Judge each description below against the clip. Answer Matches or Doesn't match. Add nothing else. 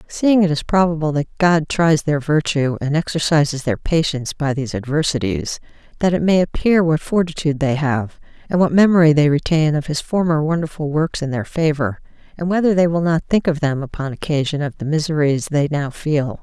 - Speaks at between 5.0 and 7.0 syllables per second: Matches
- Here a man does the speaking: Doesn't match